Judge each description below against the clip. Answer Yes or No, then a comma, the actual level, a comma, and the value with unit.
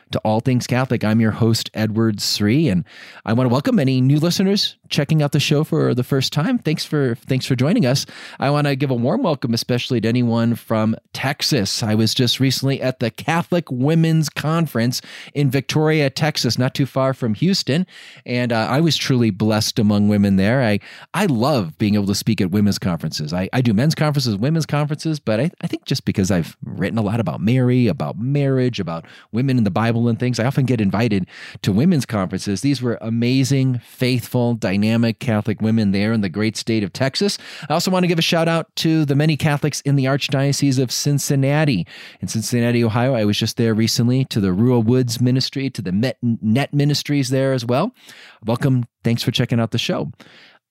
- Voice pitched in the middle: No, low, 125 Hz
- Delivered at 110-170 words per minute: No, fast, 205 wpm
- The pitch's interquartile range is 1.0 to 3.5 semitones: No, average, 4.3 semitones